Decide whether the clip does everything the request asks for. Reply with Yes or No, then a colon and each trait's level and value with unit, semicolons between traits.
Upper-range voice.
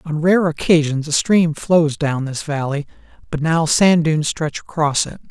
No: medium, 155 Hz